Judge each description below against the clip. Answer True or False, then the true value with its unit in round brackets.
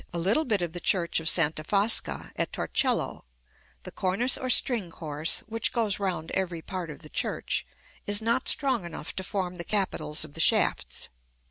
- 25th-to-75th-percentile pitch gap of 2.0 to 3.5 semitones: False (4.7 semitones)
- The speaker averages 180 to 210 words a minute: True (185 wpm)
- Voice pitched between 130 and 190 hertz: True (185 Hz)